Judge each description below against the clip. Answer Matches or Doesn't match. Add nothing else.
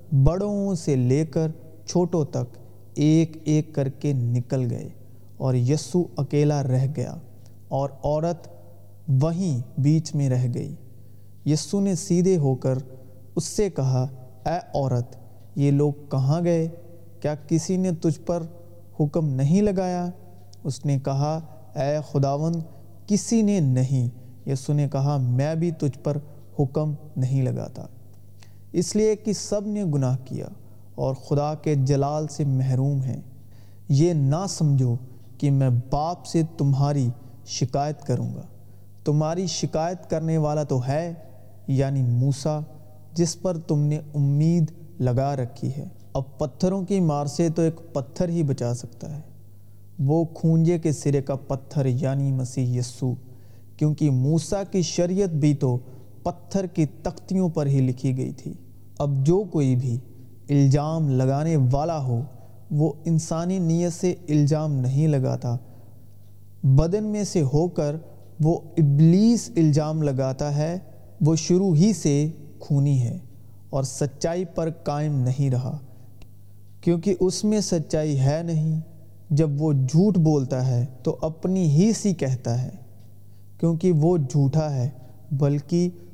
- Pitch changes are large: Doesn't match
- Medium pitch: Matches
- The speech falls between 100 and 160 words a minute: Matches